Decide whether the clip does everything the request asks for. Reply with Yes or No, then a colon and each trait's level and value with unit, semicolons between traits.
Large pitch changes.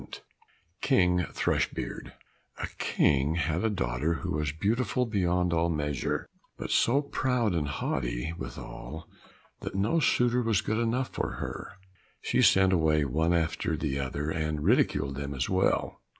Yes: wide, 6.1 semitones